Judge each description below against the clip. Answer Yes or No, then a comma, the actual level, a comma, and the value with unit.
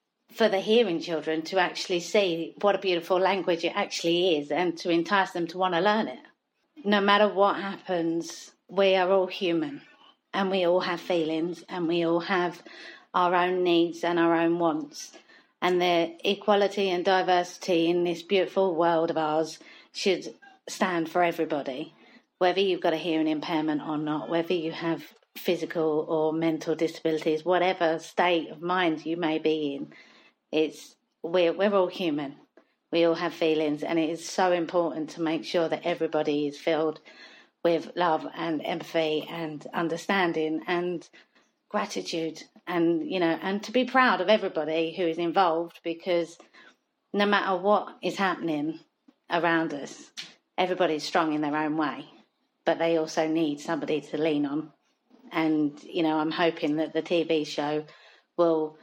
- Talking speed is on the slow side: No, average, 160 wpm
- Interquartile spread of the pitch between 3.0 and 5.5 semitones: No, narrow, 2.6 semitones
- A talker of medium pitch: Yes, medium, 170 Hz